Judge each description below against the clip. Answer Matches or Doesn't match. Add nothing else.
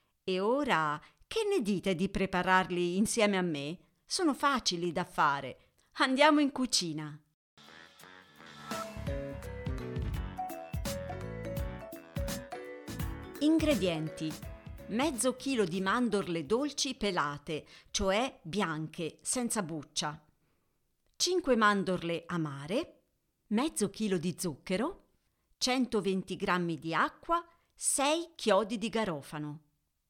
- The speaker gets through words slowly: Matches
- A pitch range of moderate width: Doesn't match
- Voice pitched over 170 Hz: Matches